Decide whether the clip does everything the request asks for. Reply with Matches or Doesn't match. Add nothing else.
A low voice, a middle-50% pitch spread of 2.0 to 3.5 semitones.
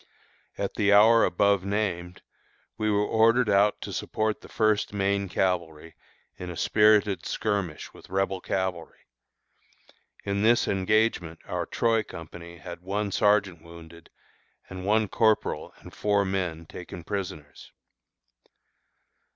Matches